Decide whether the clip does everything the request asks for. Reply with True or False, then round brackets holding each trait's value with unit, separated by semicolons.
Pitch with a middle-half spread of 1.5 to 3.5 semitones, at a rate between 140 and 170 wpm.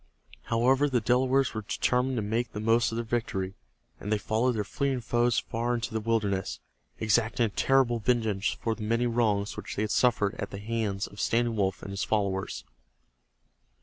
False (2.7 semitones; 185 wpm)